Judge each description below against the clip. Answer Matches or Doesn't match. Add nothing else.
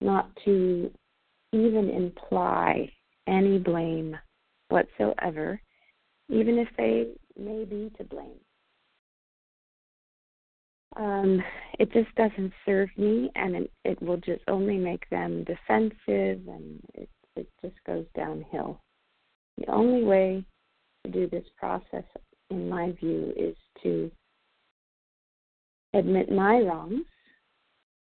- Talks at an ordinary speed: Doesn't match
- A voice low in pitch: Doesn't match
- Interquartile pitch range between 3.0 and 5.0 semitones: Doesn't match